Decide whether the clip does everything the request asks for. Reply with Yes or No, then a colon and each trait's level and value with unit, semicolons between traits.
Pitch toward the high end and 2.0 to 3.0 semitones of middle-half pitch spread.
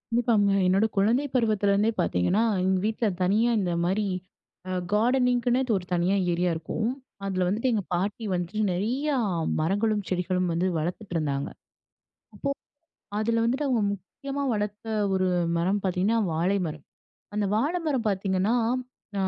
No: high, 205 Hz; average, 3.9 semitones